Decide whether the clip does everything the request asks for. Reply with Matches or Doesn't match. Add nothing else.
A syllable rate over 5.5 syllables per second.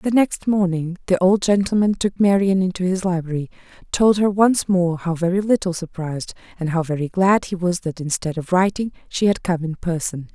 Doesn't match